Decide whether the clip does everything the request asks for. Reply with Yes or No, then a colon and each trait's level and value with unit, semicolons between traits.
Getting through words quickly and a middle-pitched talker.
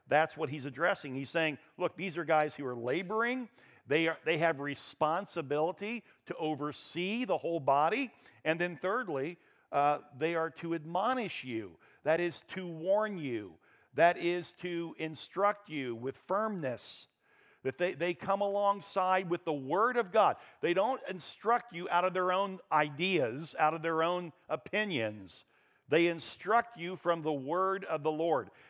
No: average, 160 wpm; medium, 170 Hz